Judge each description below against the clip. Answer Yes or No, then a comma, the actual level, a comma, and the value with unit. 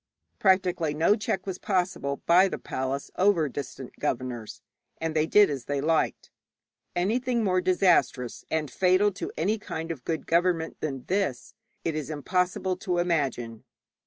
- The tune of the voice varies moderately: Yes, average, 4.6 semitones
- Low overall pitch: No, medium, 170 Hz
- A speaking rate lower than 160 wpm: Yes, average, 150 wpm